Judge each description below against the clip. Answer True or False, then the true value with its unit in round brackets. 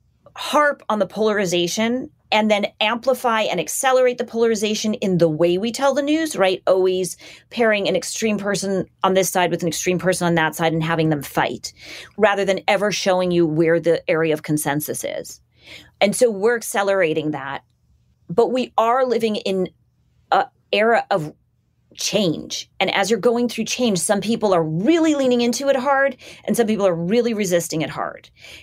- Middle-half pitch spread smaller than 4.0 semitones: False (5.2 semitones)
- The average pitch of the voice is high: True (200 Hz)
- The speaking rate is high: False (180 wpm)